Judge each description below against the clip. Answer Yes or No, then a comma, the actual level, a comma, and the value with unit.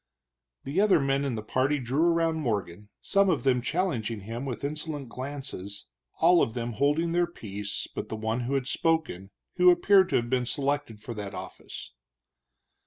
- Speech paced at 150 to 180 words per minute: Yes, average, 175 wpm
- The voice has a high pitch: No, low, 135 Hz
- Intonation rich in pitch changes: Yes, wide, 6.2 semitones